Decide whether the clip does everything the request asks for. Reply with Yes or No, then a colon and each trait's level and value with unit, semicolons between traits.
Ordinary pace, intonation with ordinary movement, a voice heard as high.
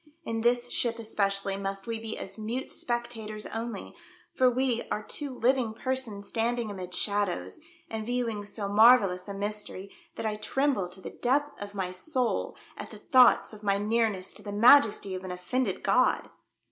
Yes: average, 170 wpm; average, 3.3 semitones; high, 220 Hz